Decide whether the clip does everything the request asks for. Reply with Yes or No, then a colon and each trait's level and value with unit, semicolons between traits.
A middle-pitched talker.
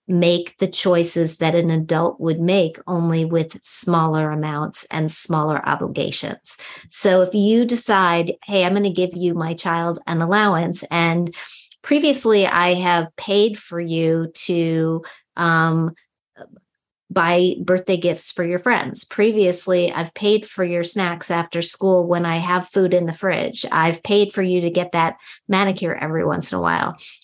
Yes: medium, 175 Hz